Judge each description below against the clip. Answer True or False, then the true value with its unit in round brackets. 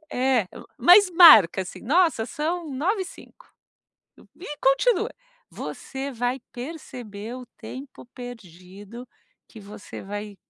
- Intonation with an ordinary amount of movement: False (7.1 semitones)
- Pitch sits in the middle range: False (255 Hz)